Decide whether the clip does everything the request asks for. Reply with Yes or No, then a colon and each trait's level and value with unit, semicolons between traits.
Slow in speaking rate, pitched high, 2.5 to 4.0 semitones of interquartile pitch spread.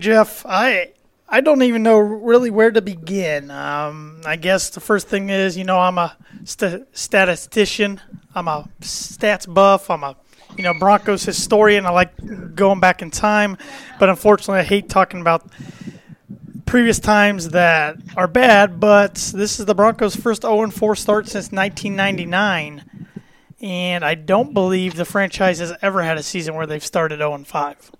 No: average, 160 wpm; high, 195 Hz; average, 3.1 semitones